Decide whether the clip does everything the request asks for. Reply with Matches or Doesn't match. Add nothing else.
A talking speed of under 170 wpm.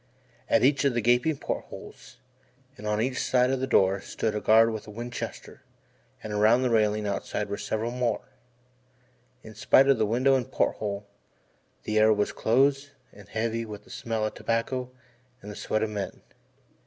Doesn't match